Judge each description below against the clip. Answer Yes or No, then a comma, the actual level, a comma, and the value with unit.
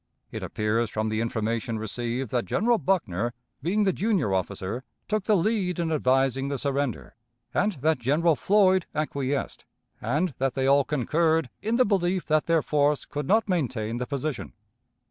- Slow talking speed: No, average, 165 wpm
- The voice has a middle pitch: Yes, medium, 145 Hz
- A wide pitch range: Yes, wide, 6.7 semitones